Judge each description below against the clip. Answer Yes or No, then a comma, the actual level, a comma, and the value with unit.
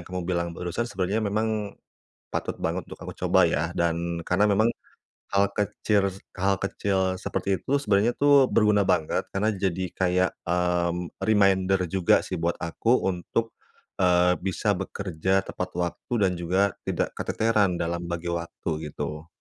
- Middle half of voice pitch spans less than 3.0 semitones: Yes, narrow, 2.6 semitones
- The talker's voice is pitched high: No, very low, 95 Hz